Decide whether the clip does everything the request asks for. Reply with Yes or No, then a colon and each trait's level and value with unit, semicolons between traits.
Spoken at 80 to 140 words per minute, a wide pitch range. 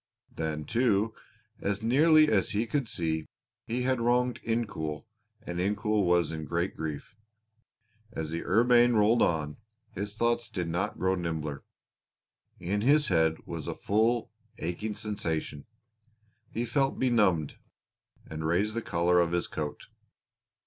Yes: slow, 135 wpm; wide, 6.0 semitones